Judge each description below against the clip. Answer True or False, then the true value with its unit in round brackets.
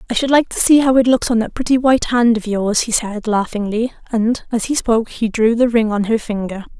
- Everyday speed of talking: False (255 wpm)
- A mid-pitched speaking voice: False (230 Hz)